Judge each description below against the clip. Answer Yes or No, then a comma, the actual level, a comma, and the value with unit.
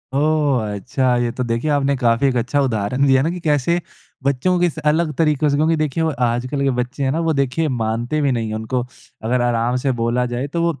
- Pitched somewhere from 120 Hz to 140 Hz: Yes, low, 135 Hz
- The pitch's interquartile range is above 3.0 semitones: Yes, average, 3.9 semitones